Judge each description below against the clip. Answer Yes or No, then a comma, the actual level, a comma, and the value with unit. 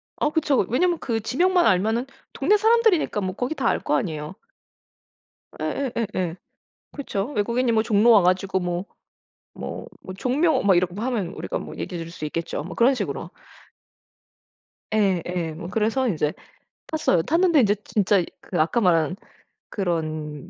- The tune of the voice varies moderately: No, wide, 6.5 semitones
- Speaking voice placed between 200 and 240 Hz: Yes, high, 205 Hz